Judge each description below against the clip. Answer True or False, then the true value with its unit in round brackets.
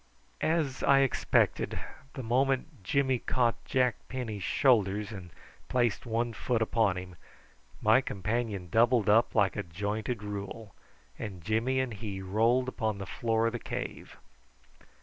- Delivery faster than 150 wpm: False (140 wpm)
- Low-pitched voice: True (115 Hz)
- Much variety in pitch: False (3.5 semitones)